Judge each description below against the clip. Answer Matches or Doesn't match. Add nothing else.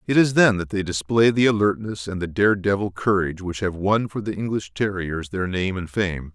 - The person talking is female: Doesn't match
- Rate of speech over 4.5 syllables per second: Matches